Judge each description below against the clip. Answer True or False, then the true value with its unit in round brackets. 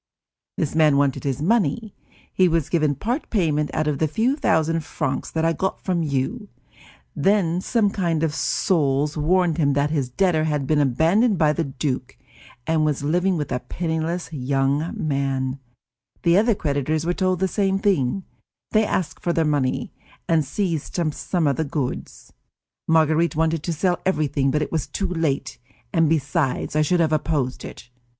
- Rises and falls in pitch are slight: False (3.7 semitones)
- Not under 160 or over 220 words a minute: True (170 wpm)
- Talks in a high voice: False (160 Hz)